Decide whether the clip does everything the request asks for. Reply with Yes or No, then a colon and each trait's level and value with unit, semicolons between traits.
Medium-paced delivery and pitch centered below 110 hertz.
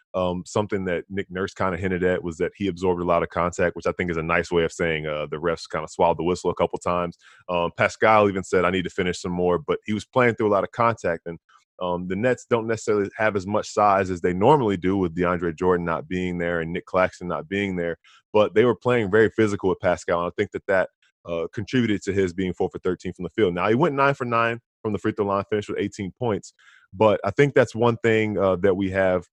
No: fast, 270 wpm; very low, 95 Hz